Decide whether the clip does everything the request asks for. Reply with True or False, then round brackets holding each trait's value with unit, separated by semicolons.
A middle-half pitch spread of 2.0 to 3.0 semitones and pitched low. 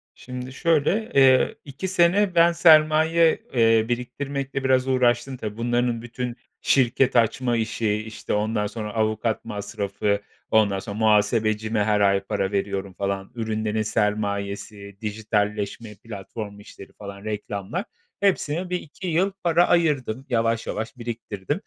False (4.4 semitones; 115 Hz)